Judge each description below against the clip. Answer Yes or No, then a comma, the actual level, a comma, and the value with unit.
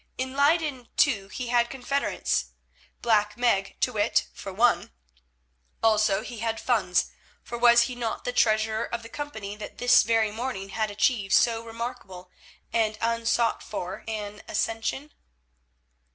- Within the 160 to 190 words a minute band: No, average, 140 wpm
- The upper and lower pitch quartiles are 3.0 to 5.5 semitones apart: No, narrow, 2.5 semitones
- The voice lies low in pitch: No, high, 225 Hz